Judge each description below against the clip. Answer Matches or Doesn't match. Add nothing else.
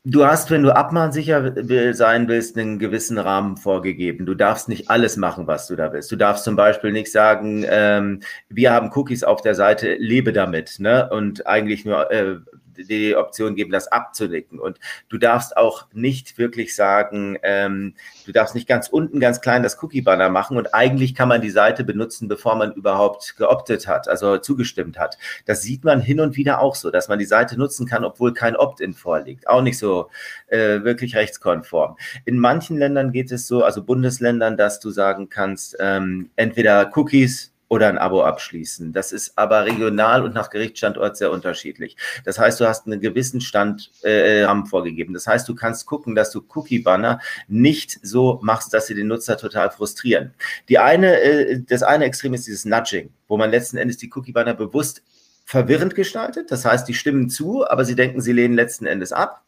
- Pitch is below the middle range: Matches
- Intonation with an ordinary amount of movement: Matches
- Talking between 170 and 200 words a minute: Matches